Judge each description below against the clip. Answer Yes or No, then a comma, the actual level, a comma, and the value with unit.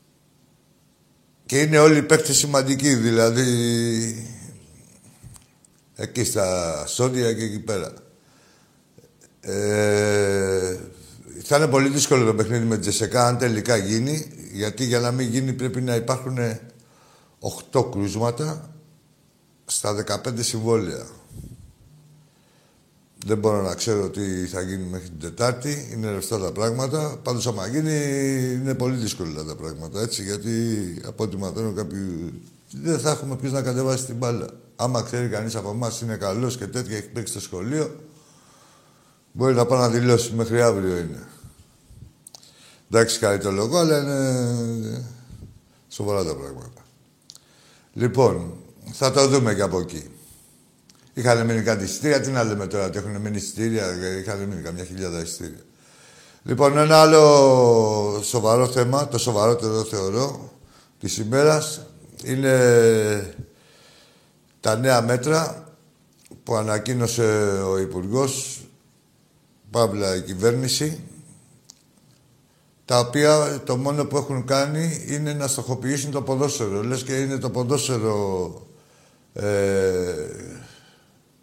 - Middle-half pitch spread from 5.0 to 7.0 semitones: No, average, 4.4 semitones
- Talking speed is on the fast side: No, average, 125 wpm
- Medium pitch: No, low, 120 Hz